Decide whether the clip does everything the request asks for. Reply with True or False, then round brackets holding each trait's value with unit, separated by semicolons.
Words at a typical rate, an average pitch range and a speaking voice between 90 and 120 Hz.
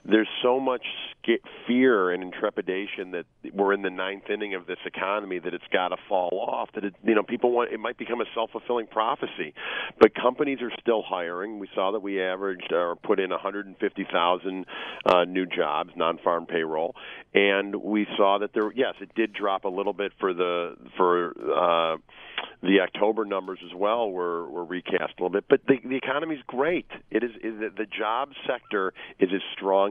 True (195 wpm; 3.4 semitones; 100 Hz)